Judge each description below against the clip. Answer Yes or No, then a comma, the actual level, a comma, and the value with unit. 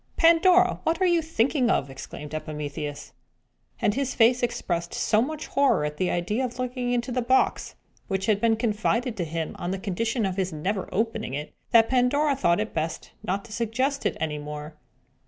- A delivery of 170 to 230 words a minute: Yes, average, 190 wpm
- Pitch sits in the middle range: No, high, 225 Hz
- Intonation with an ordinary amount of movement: No, wide, 6.8 semitones